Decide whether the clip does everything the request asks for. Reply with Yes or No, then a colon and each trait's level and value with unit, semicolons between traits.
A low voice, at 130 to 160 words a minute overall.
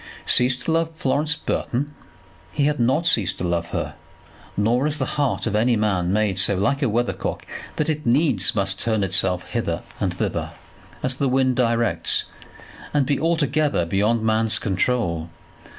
No: low, 120 Hz; average, 170 wpm